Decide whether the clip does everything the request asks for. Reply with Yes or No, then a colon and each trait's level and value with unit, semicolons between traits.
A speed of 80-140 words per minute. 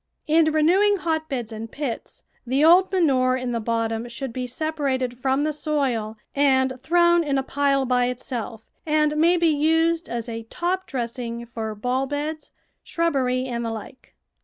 No: average, 160 wpm